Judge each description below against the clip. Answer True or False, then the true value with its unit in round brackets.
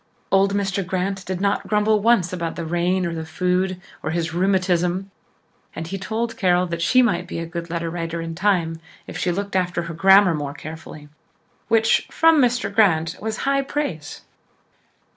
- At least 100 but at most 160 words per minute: False (180 wpm)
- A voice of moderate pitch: True (180 Hz)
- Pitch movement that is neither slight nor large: True (3.1 semitones)